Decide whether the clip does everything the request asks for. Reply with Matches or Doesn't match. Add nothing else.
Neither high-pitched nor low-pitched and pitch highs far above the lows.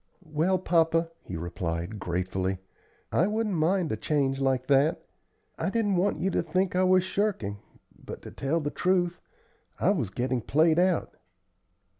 Matches